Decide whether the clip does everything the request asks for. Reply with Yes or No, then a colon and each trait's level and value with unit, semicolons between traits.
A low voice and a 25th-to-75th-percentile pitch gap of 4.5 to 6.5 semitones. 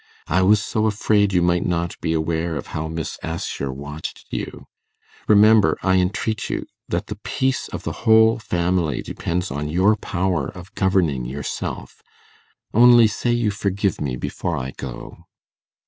Yes: very low, 90 Hz; average, 4.8 semitones